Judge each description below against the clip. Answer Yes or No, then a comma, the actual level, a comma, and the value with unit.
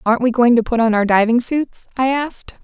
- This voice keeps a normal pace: No, fast, 250 wpm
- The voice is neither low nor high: No, high, 240 Hz